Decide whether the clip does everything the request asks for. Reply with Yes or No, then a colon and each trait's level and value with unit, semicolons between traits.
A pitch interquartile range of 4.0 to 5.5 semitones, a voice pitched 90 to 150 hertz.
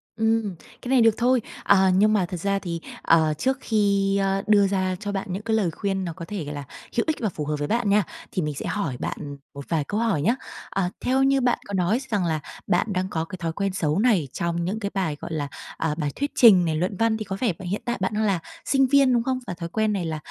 No: average, 4.6 semitones; high, 195 Hz